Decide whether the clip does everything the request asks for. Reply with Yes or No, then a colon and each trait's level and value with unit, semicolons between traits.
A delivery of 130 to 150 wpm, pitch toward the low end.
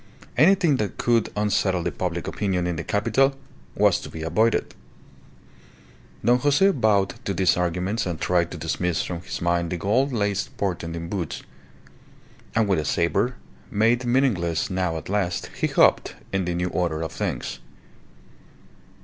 No: average, 160 wpm; very low, 95 Hz